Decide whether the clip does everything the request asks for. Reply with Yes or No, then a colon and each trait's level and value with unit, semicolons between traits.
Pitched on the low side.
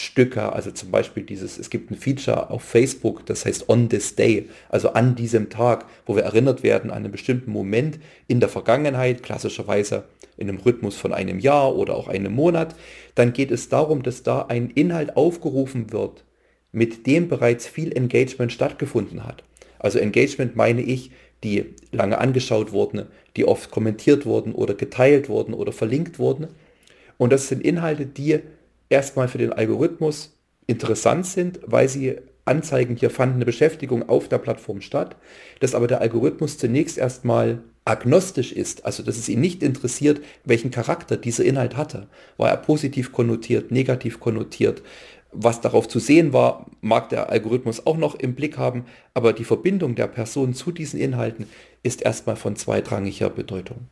Yes: low, 125 Hz